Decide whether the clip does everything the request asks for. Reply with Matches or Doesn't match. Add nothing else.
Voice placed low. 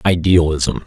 Matches